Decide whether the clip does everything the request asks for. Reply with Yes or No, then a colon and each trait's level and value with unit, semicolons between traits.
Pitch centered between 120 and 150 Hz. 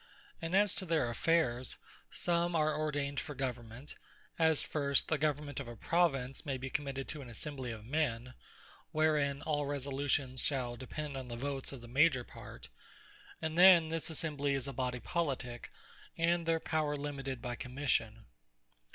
Yes: medium, 140 Hz